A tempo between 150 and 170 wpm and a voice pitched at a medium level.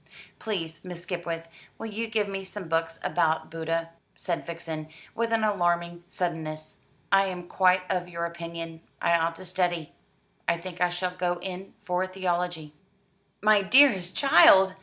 Yes: average, 155 wpm; medium, 175 Hz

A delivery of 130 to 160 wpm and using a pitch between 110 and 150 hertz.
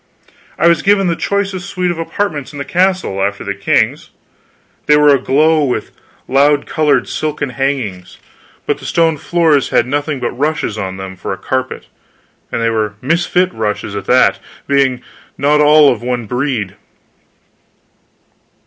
Yes: average, 155 wpm; medium, 140 Hz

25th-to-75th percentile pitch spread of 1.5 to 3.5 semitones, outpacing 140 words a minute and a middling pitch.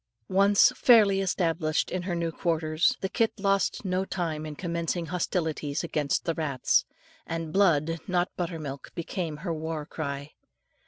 Yes: average, 3.0 semitones; average, 150 wpm; medium, 170 Hz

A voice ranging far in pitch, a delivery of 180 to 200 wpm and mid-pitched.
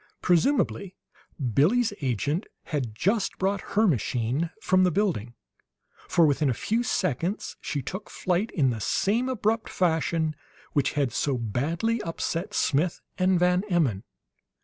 No: wide, 6.2 semitones; slow, 135 wpm; medium, 170 Hz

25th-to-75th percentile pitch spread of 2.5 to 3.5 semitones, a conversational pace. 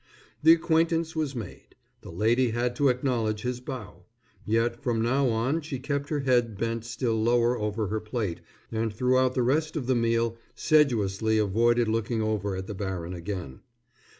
Yes: average, 3.2 semitones; average, 170 wpm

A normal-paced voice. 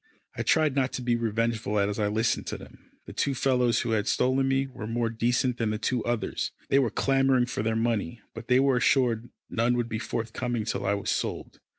No: fast, 220 wpm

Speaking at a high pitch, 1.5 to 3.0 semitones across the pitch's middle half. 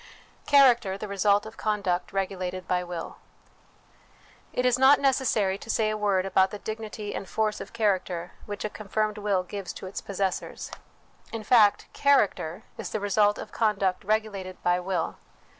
Yes: high, 205 Hz; narrow, 2.4 semitones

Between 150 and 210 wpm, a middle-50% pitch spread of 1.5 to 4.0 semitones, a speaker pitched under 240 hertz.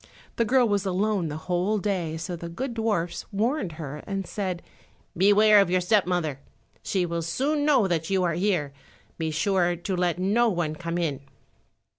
Yes: average, 180 wpm; average, 3.7 semitones; medium, 185 Hz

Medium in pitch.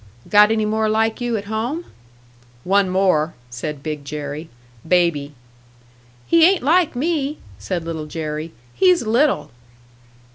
No: high, 200 Hz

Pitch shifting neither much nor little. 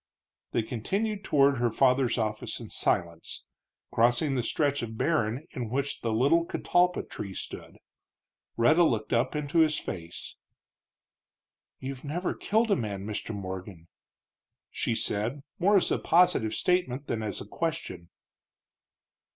No: wide, 6.4 semitones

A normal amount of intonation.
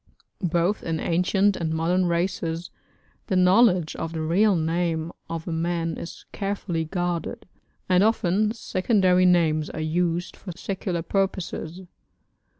No: narrow, 2.3 semitones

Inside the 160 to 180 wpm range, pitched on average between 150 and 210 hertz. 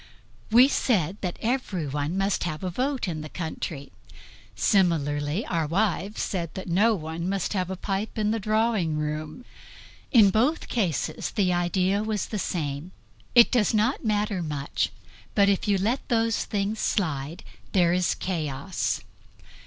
No: average, 150 wpm; high, 190 Hz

